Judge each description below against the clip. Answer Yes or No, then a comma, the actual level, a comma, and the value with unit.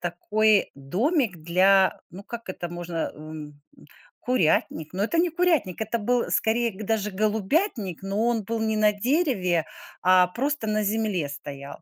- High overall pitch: Yes, high, 205 Hz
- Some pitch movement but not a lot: Yes, average, 4.7 semitones